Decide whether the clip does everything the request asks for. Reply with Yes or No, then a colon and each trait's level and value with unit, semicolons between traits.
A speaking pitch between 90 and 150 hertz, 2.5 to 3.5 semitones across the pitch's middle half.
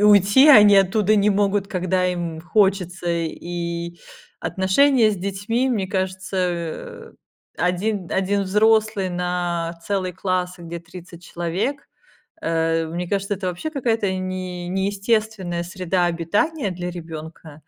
No: medium, 185 Hz; average, 2.8 semitones